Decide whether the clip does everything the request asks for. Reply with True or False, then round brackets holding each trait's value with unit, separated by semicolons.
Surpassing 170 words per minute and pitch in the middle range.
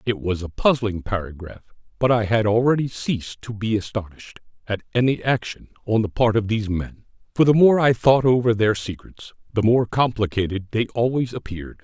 False (185 wpm; 110 Hz)